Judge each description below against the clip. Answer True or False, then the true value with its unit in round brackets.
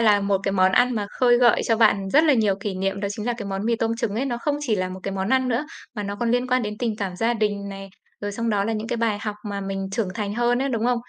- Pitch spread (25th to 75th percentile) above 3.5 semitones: False (3.1 semitones)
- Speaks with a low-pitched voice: False (215 Hz)